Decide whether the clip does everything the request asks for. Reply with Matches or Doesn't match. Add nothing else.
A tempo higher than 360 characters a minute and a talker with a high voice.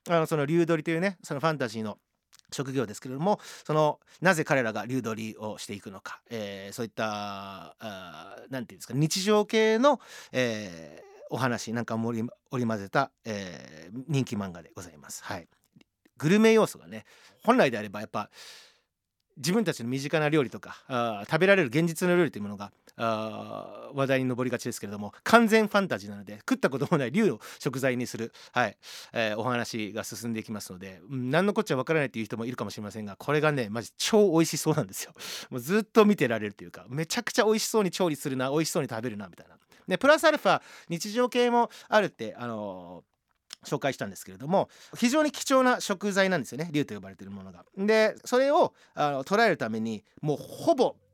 Doesn't match